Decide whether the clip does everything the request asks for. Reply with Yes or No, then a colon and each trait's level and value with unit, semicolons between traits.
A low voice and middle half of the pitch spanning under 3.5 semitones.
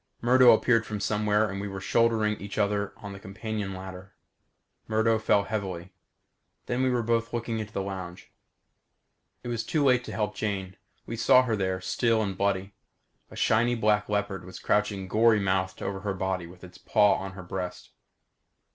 Yes: low, 105 Hz; average, 2.7 semitones